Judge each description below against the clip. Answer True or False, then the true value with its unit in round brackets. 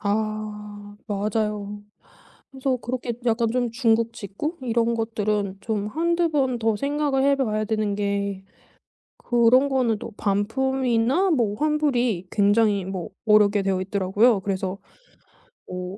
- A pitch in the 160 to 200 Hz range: False (220 Hz)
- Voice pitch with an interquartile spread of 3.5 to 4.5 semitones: True (3.8 semitones)